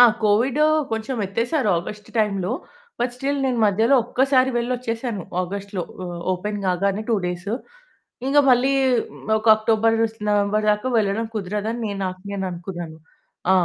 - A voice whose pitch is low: No, high, 215 Hz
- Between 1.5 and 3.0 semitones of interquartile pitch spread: No, average, 3.6 semitones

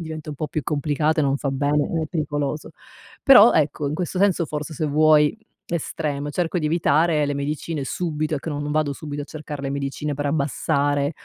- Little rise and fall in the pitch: Yes, narrow, 1.6 semitones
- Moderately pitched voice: Yes, medium, 150 Hz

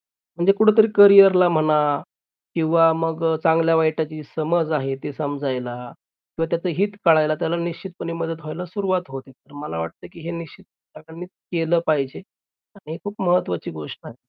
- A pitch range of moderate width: No, narrow, 2.3 semitones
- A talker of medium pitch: Yes, medium, 165 Hz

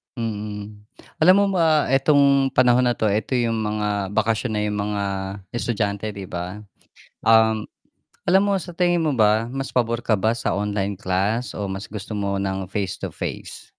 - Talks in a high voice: No, low, 110 Hz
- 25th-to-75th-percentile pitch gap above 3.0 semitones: Yes, average, 3.7 semitones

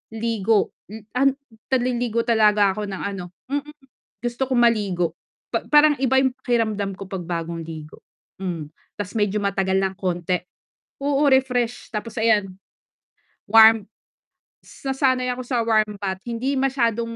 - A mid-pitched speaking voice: No, high, 220 Hz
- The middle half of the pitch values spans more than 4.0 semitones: Yes, average, 4.4 semitones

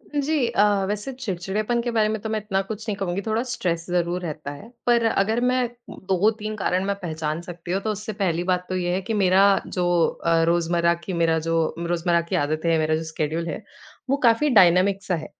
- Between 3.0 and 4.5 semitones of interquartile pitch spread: Yes, average, 4.1 semitones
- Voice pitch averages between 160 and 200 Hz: Yes, medium, 185 Hz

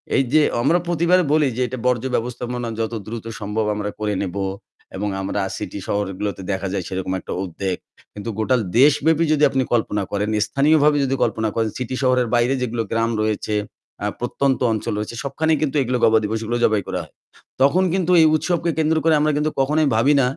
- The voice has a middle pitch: No, low, 120 Hz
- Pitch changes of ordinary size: No, wide, 5.8 semitones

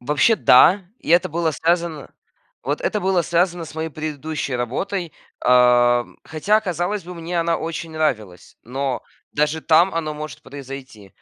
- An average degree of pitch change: Yes, average, 4.1 semitones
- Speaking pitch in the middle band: Yes, medium, 155 Hz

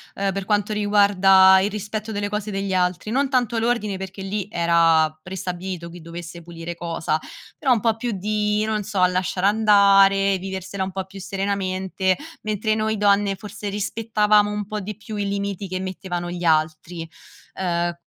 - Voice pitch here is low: No, high, 195 Hz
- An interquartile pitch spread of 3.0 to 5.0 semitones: No, narrow, 2.4 semitones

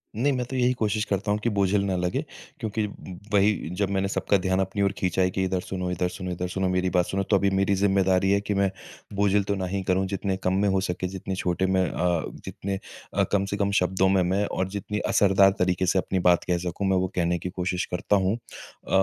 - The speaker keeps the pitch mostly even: Yes, narrow, 1.5 semitones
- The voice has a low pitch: Yes, very low, 95 Hz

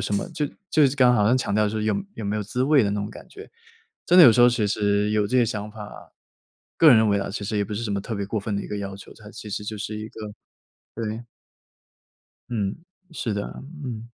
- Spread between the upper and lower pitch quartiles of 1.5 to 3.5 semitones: Yes, average, 2.8 semitones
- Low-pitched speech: Yes, low, 110 Hz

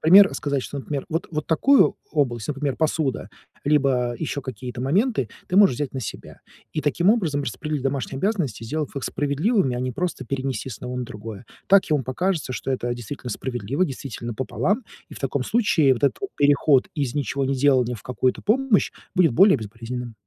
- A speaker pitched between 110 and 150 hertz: Yes, medium, 140 Hz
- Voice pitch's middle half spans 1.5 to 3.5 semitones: No, average, 4.1 semitones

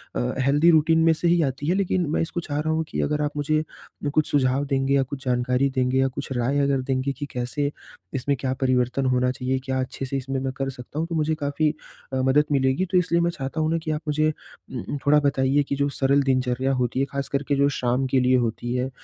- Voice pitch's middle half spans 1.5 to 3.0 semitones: Yes, narrow, 2.4 semitones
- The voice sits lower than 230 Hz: Yes, medium, 140 Hz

